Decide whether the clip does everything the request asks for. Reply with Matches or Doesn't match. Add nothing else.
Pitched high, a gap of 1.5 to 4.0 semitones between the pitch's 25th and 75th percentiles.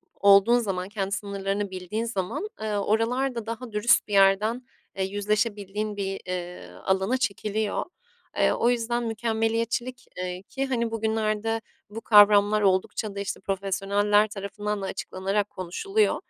Matches